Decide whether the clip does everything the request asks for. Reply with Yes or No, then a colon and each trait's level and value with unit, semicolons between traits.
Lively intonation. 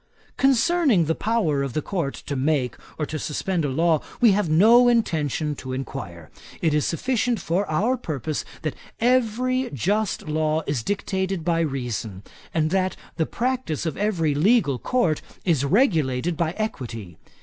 Yes: wide, 6.9 semitones